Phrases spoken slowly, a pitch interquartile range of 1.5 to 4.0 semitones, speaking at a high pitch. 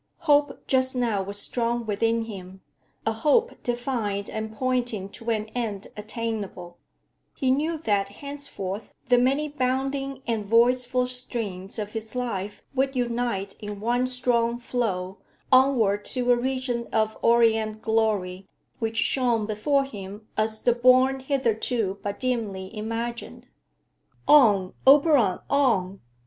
Yes: slow, 130 wpm; average, 3.5 semitones; high, 230 Hz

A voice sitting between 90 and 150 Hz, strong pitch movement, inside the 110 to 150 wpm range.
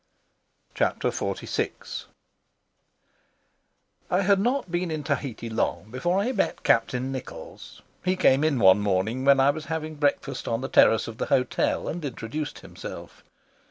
Yes: medium, 140 Hz; wide, 6.2 semitones; average, 140 wpm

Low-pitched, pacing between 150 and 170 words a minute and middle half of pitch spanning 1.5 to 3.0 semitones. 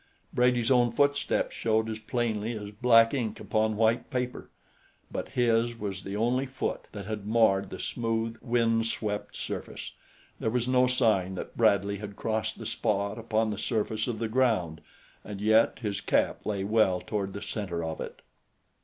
Yes: low, 110 Hz; average, 165 wpm; narrow, 2.4 semitones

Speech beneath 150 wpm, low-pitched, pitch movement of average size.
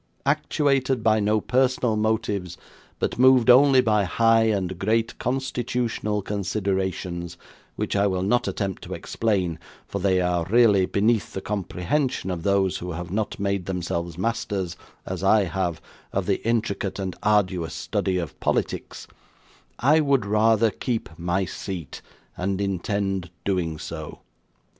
Yes: average, 140 wpm; low, 100 Hz; average, 3.6 semitones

